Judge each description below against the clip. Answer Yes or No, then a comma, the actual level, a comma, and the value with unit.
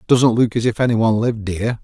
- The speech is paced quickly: Yes, fast, 260 wpm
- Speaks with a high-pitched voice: No, low, 115 Hz